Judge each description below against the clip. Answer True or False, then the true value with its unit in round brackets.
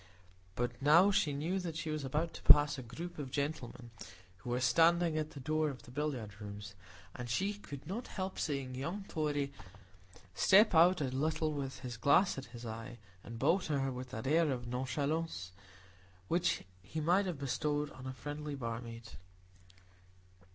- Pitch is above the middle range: False (145 Hz)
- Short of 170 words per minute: False (175 wpm)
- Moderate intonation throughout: True (4.5 semitones)